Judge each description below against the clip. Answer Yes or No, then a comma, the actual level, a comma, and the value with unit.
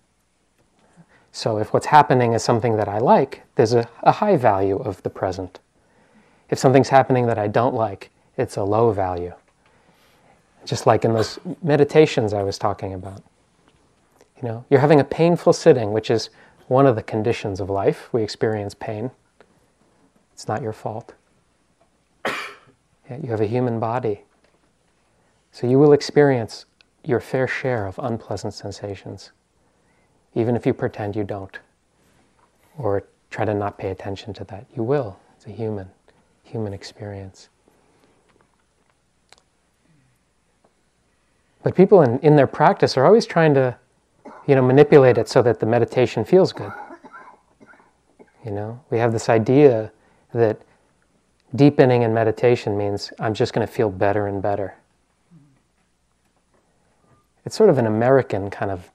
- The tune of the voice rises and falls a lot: No, average, 4.5 semitones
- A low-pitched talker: Yes, low, 115 Hz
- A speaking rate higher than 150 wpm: No, average, 145 wpm